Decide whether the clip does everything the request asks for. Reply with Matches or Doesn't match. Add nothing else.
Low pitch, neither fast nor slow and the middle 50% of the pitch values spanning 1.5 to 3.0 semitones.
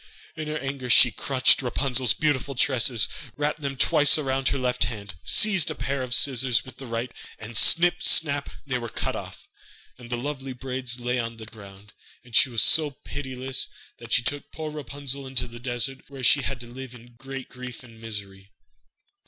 Matches